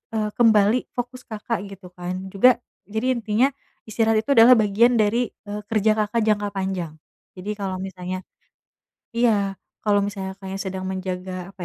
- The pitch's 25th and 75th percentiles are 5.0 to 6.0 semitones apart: No, average, 2.8 semitones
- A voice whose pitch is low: No, high, 205 Hz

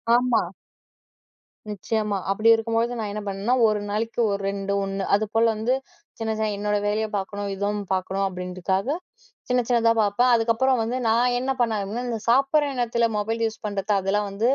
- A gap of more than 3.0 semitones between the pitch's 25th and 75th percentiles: No, average, 2.7 semitones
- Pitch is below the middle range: No, high, 220 Hz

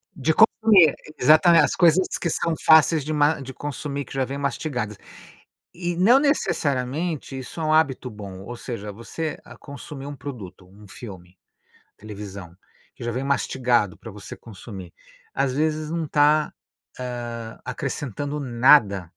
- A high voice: No, low, 135 Hz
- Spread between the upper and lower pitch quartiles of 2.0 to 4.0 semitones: No, average, 5.1 semitones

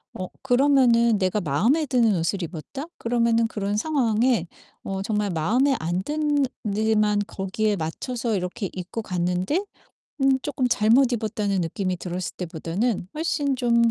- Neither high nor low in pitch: No, high, 215 Hz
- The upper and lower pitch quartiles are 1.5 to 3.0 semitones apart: No, average, 5.3 semitones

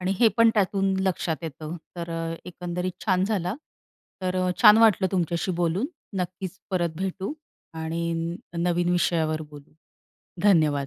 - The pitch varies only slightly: Yes, narrow, 2.2 semitones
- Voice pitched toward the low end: No, medium, 180 Hz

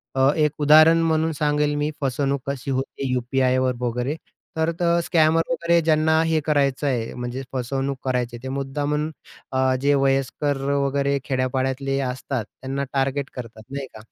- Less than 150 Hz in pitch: Yes, medium, 140 Hz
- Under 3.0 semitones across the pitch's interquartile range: Yes, narrow, 2.4 semitones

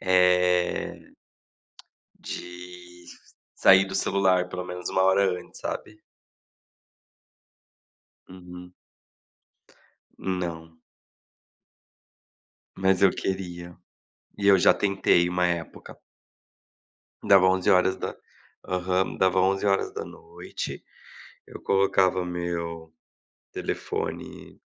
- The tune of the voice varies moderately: No, narrow, 1.3 semitones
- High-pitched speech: No, very low, 90 Hz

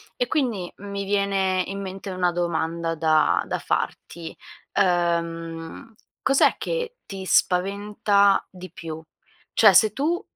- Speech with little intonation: No, average, 3.2 semitones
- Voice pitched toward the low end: No, high, 190 Hz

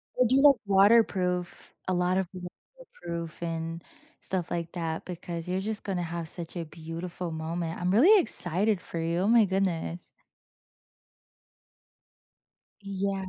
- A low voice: No, medium, 180 Hz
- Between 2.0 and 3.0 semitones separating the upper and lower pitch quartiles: Yes, average, 2.7 semitones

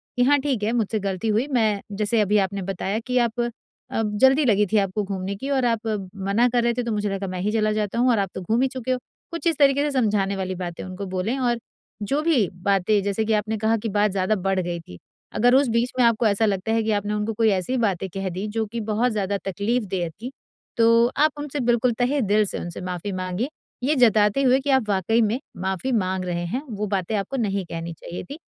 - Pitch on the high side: Yes, high, 210 Hz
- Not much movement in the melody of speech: No, average, 3.8 semitones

